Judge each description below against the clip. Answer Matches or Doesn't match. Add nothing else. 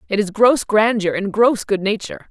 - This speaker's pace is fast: Matches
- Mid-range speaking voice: Doesn't match